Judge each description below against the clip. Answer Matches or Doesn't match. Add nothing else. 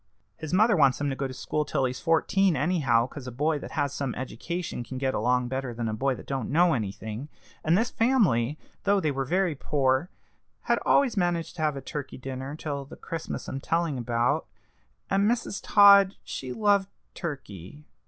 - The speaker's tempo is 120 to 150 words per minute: Doesn't match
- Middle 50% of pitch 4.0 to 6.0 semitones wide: Matches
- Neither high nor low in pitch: Matches